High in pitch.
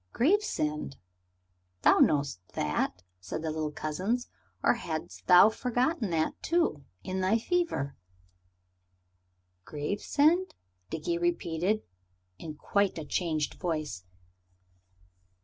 No: medium, 180 Hz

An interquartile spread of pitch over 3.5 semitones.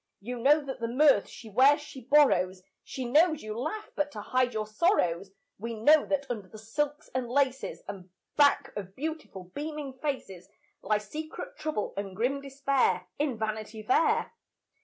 Yes: wide, 5.4 semitones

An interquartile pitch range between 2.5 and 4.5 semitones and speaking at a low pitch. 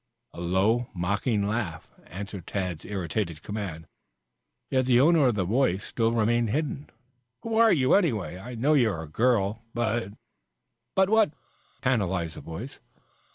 No: average, 5.2 semitones; low, 110 Hz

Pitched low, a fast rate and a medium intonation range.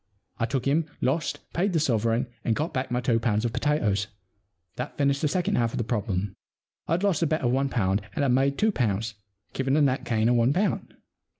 Yes: low, 130 Hz; fast, 220 wpm; average, 4.6 semitones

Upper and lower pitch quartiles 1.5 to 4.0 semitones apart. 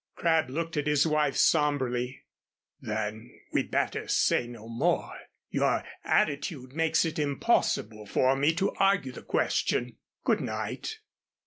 No: average, 4.7 semitones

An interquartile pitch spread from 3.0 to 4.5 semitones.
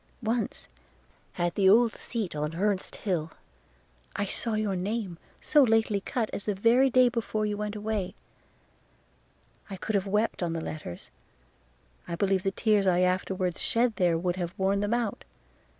Yes: average, 3.3 semitones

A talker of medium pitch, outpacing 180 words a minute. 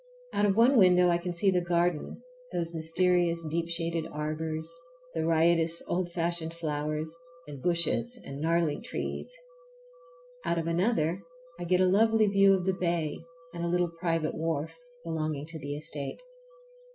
No: medium, 170 Hz; average, 155 wpm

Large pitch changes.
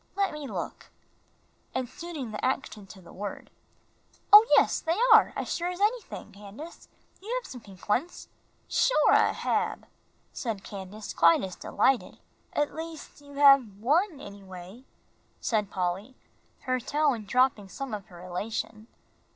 Yes: wide, 7.1 semitones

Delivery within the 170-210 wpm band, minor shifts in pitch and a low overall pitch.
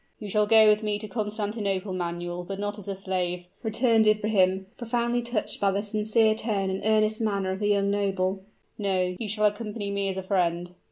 No: average, 200 wpm; narrow, 2.1 semitones; high, 205 Hz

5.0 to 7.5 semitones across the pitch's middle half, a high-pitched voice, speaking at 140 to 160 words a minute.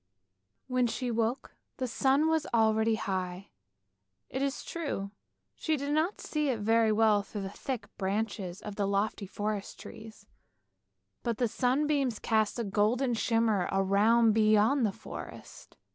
No: average, 3.6 semitones; high, 225 Hz; average, 145 wpm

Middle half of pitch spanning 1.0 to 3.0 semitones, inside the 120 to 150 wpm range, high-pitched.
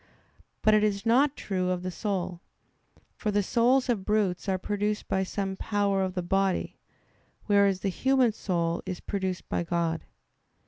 No: narrow, 2.5 semitones; average, 165 wpm; high, 195 Hz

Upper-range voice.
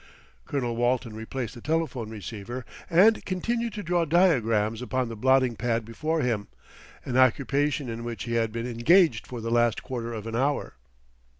No: low, 120 Hz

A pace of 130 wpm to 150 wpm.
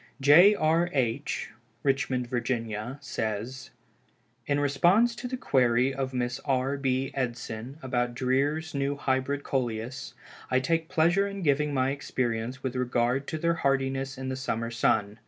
Yes: average, 145 wpm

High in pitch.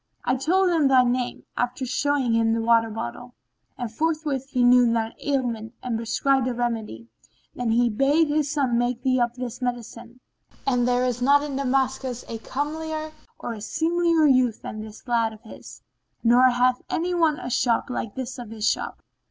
Yes: very high, 250 Hz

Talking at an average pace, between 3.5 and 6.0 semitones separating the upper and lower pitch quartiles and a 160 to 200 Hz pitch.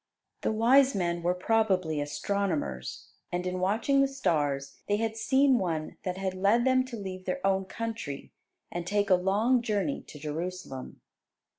Yes: average, 160 wpm; average, 4.7 semitones; high, 190 Hz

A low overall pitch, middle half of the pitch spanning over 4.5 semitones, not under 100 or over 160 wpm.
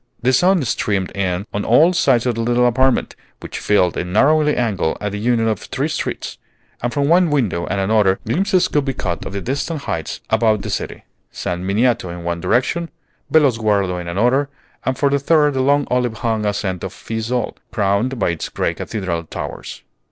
No: low, 115 Hz; wide, 5.5 semitones; average, 190 wpm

